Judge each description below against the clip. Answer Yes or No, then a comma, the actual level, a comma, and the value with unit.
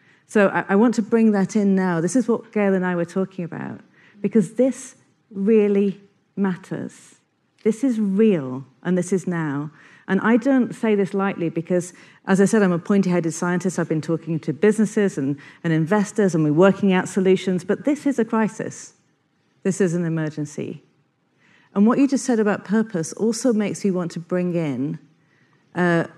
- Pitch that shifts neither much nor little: Yes, average, 4.2 semitones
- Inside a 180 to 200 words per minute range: Yes, average, 185 wpm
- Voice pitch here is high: Yes, high, 195 Hz